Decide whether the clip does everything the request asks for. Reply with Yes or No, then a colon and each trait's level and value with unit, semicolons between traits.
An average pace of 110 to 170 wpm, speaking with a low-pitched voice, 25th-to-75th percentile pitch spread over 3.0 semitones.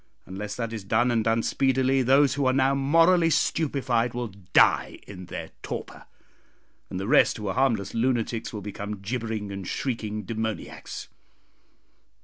Yes: average, 150 wpm; low, 115 Hz; average, 4.0 semitones